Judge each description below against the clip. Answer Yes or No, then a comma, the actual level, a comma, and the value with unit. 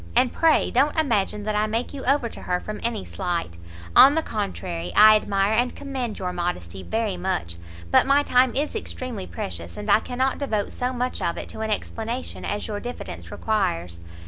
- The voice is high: Yes, high, 215 Hz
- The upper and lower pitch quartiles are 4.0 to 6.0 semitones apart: Yes, average, 4.9 semitones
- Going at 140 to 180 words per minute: No, average, 195 wpm